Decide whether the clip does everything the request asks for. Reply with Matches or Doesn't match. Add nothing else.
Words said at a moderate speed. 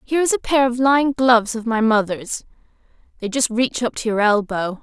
Doesn't match